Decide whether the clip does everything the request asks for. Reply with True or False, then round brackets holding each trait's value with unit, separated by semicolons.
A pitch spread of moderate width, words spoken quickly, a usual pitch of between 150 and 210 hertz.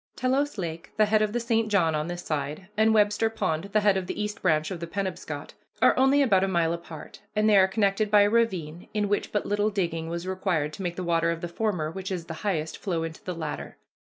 True (4.0 semitones; 245 wpm; 190 Hz)